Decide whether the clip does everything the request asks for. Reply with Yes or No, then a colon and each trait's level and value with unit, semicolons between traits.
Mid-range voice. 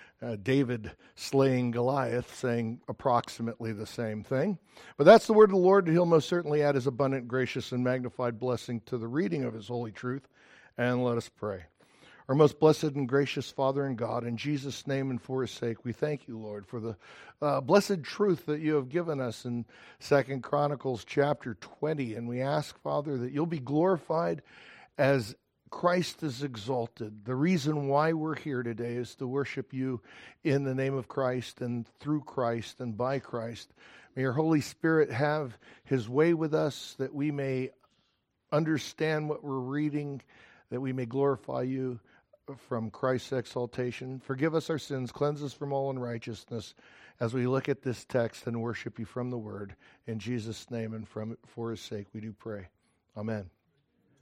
No: low, 130 Hz